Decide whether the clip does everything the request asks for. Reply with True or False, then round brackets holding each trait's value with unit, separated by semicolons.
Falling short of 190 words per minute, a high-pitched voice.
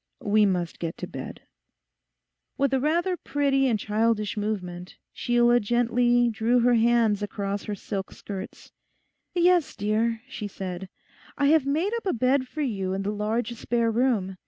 True (160 wpm; 230 Hz)